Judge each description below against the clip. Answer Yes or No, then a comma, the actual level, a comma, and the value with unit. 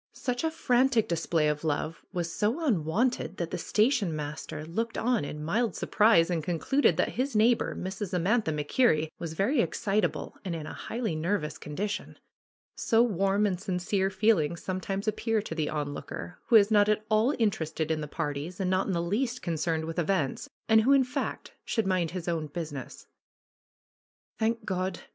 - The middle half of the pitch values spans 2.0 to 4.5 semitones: No, wide, 5.5 semitones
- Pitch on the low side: No, high, 190 Hz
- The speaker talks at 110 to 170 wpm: No, average, 180 wpm